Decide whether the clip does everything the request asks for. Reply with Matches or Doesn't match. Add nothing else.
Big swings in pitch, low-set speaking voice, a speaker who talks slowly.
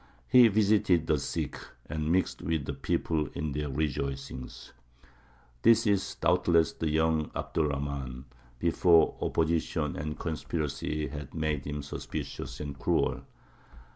Doesn't match